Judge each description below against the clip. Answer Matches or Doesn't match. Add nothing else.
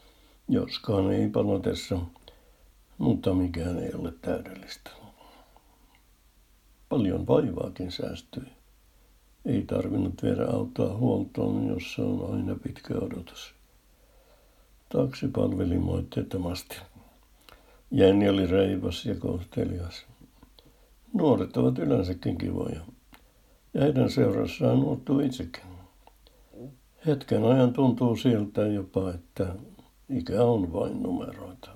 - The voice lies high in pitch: Doesn't match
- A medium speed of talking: Doesn't match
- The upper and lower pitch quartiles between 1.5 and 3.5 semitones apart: Doesn't match